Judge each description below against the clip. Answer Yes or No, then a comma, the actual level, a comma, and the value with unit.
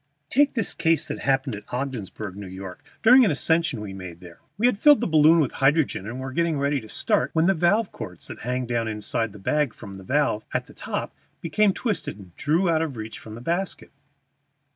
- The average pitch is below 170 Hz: Yes, low, 135 Hz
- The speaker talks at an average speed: No, fast, 225 wpm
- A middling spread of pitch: No, wide, 7.5 semitones